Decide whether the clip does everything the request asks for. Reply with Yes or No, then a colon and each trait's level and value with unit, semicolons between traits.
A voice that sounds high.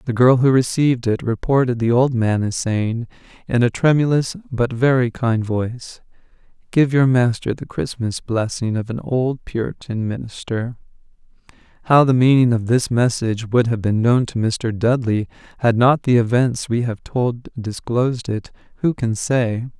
No: low, 120 Hz